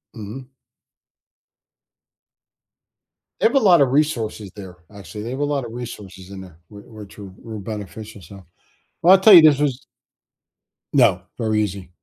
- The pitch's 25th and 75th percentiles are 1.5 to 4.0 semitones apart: No, wide, 5.6 semitones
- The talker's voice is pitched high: No, low, 110 Hz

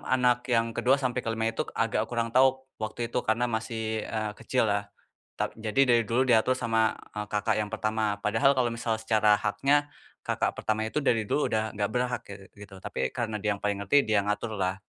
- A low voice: Yes, low, 110 Hz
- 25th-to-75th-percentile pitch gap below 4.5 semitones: Yes, narrow, 2.6 semitones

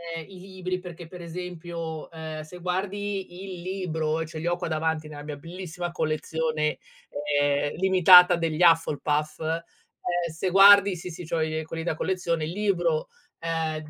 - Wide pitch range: No, narrow, 2.4 semitones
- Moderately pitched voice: Yes, medium, 165 Hz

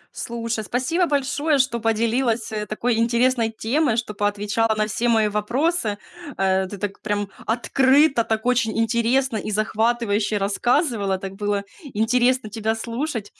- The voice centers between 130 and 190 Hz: No, high, 225 Hz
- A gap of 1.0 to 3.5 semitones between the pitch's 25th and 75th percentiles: Yes, average, 3.0 semitones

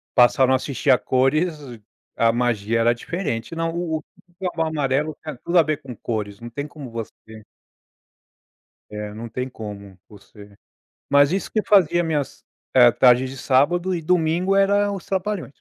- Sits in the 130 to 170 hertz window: Yes, medium, 140 Hz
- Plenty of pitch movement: Yes, wide, 6.4 semitones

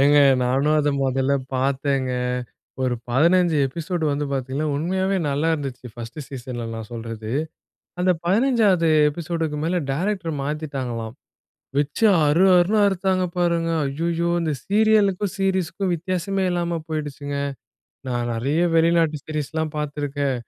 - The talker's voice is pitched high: No, medium, 155 Hz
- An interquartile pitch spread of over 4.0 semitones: Yes, average, 4.5 semitones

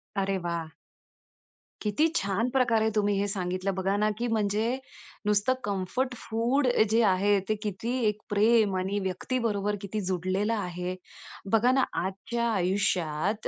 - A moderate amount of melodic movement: Yes, average, 3.0 semitones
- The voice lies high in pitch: Yes, high, 205 Hz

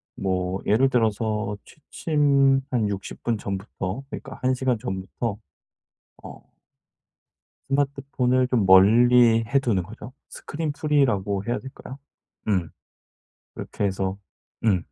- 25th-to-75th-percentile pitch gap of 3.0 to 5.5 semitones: Yes, average, 5.2 semitones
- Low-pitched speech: Yes, low, 115 Hz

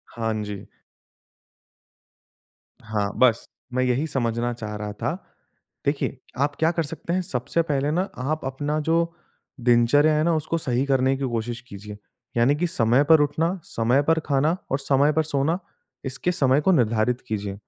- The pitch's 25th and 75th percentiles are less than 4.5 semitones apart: No, average, 4.8 semitones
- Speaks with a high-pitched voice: No, low, 135 Hz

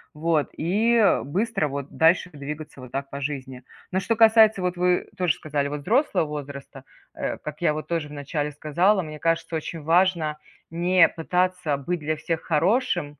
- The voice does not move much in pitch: No, average, 3.7 semitones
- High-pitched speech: No, medium, 160 Hz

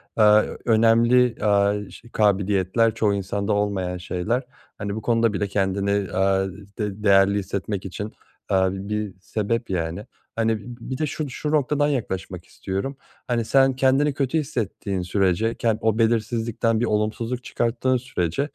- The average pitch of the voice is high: No, low, 105 Hz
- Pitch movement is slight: No, average, 3.2 semitones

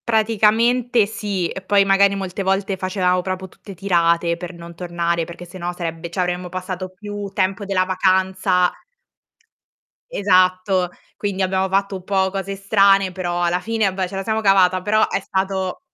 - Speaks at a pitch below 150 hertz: No, high, 190 Hz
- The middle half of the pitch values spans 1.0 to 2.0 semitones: Yes, narrow, 1.6 semitones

